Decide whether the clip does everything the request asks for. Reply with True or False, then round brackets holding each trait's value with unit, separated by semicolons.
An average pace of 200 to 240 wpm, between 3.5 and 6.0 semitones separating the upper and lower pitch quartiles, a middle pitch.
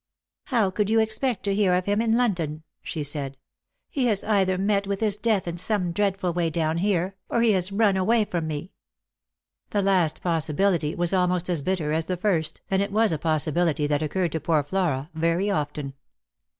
True (205 wpm; 4.1 semitones; 180 Hz)